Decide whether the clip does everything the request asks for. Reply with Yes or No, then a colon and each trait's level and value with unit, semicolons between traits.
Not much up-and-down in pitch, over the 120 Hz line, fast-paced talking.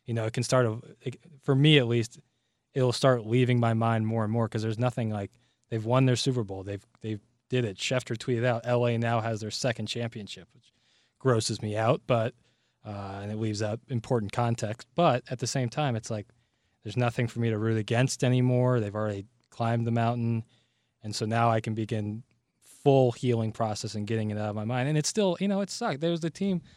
No: narrow, 2.3 semitones; low, 115 Hz; fast, 220 wpm